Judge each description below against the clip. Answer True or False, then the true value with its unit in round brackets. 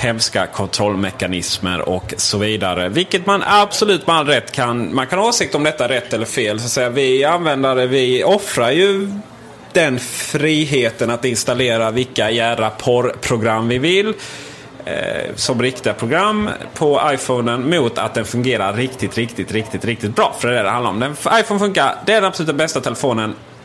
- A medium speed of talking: True (175 wpm)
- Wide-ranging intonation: True (6.8 semitones)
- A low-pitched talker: True (125 Hz)